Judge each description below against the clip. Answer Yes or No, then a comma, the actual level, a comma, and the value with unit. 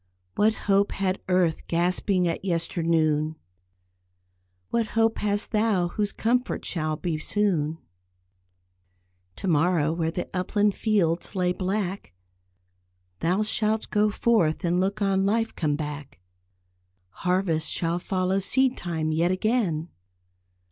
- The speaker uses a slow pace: Yes, slow, 120 wpm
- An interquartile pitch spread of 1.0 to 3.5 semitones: No, average, 4.0 semitones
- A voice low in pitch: No, medium, 185 Hz